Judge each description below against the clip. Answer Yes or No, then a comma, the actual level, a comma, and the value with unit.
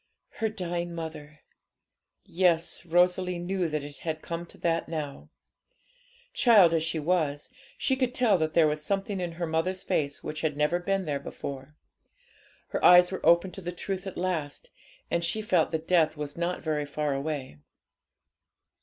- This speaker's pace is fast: No, average, 170 wpm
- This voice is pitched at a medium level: Yes, medium, 170 Hz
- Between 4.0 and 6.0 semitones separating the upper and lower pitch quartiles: No, average, 3.0 semitones